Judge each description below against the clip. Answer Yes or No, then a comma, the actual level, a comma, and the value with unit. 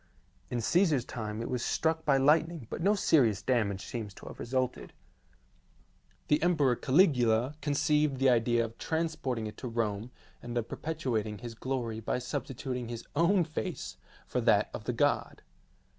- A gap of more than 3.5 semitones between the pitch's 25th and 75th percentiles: Yes, average, 4.8 semitones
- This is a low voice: Yes, low, 125 Hz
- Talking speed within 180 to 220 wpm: No, average, 160 wpm